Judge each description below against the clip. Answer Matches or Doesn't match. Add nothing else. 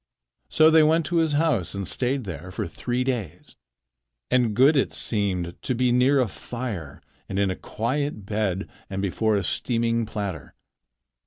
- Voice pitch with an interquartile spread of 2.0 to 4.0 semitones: Doesn't match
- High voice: Doesn't match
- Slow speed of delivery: Doesn't match